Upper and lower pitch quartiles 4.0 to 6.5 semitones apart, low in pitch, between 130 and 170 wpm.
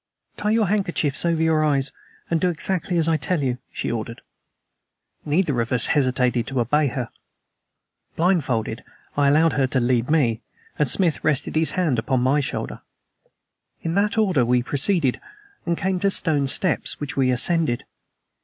No: average, 4.9 semitones; medium, 150 Hz; average, 165 wpm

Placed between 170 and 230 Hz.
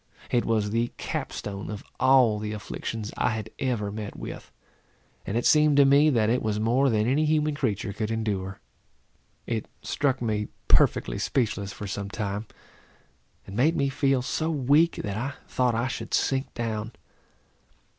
No: low, 115 Hz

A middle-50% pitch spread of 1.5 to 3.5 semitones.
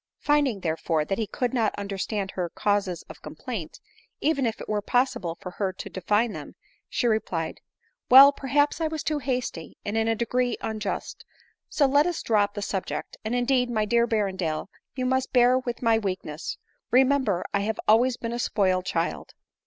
No: average, 4.5 semitones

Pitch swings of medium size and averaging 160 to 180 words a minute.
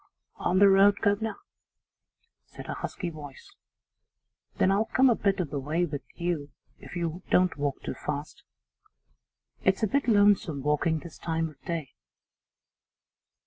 No: average, 4.8 semitones; average, 145 wpm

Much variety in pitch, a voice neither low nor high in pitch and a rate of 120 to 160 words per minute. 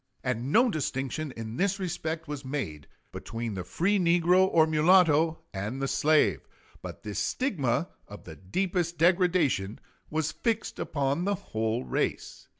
Yes: wide, 6.8 semitones; medium, 155 Hz; average, 145 wpm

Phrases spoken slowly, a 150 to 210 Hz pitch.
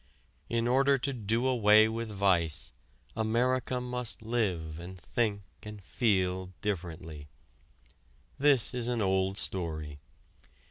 No: slow, 110 wpm; low, 105 Hz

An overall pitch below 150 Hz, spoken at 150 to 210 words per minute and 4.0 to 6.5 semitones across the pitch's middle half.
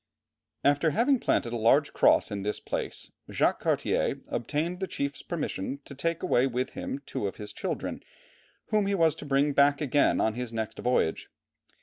Yes: medium, 140 Hz; average, 180 wpm; average, 5.0 semitones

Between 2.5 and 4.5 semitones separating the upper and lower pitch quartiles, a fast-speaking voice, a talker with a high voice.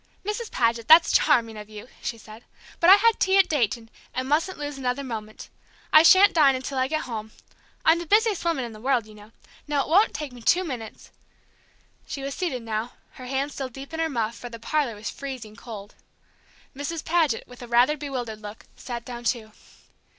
No: average, 5.2 semitones; fast, 210 wpm; very high, 260 Hz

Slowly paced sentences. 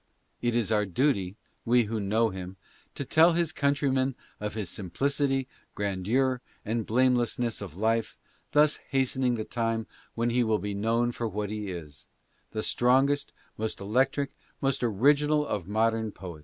No: average, 155 wpm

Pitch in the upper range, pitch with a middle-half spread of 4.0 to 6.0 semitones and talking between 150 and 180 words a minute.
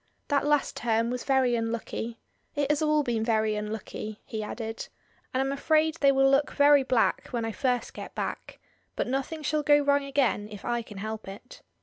No: very high, 250 Hz; average, 4.3 semitones; average, 195 wpm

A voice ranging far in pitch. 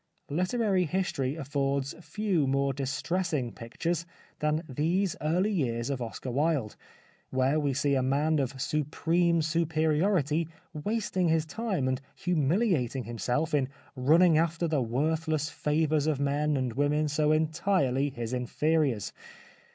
No: average, 3.6 semitones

